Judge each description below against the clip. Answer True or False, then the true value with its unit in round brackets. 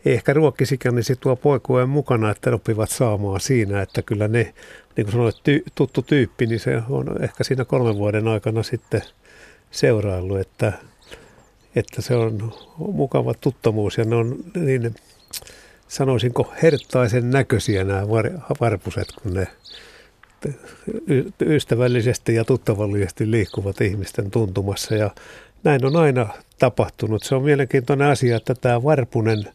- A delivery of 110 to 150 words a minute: True (135 wpm)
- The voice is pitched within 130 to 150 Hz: False (120 Hz)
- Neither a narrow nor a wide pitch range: True (3.4 semitones)